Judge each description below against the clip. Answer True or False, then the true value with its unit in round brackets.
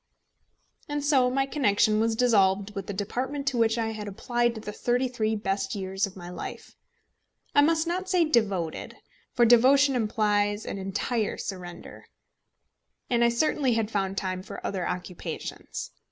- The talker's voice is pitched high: True (220 Hz)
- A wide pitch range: False (4.3 semitones)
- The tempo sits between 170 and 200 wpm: False (155 wpm)